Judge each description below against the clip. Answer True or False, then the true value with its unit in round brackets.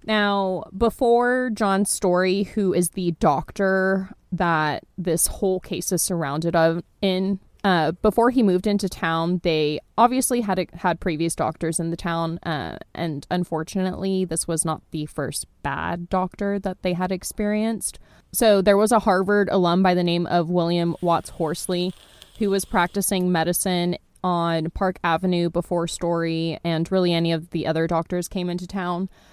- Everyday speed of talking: True (160 wpm)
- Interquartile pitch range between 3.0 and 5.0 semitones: False (2.5 semitones)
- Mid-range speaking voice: True (180 Hz)